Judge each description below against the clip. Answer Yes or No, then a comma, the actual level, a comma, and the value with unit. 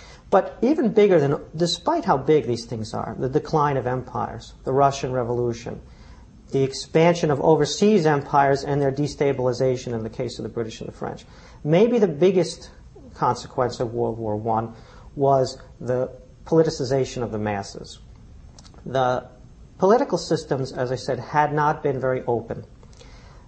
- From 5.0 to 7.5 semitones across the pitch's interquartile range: No, average, 3.7 semitones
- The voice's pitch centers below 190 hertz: Yes, low, 135 Hz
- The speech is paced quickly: No, average, 150 wpm